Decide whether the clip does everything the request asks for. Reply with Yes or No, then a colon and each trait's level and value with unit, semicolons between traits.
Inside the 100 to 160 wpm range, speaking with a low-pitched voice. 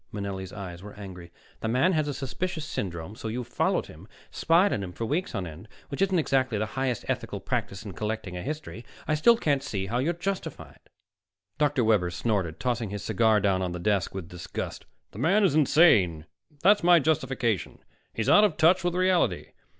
No: average, 195 wpm; low, 115 Hz